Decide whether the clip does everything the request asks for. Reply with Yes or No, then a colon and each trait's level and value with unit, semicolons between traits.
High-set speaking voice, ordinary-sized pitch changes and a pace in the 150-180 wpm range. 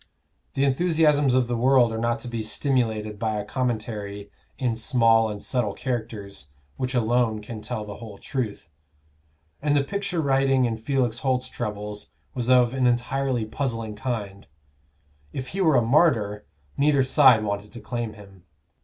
No: low, 120 Hz; average, 3.6 semitones; average, 160 wpm